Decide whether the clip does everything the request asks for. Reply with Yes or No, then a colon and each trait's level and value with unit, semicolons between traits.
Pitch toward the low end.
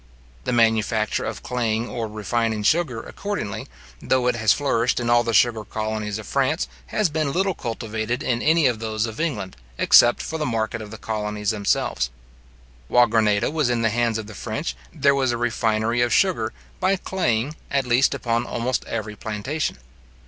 Yes: low, 115 Hz